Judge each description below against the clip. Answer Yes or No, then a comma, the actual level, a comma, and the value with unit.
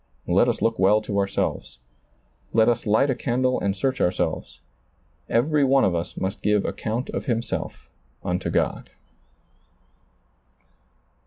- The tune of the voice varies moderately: Yes, average, 4.3 semitones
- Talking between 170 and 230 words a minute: No, slow, 135 wpm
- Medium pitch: No, low, 115 Hz